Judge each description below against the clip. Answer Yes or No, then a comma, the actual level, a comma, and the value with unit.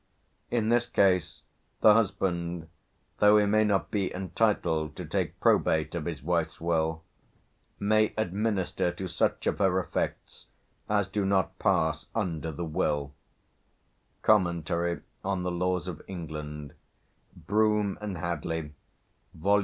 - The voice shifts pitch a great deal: No, average, 3.7 semitones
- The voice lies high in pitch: No, very low, 90 Hz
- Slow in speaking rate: Yes, slow, 130 wpm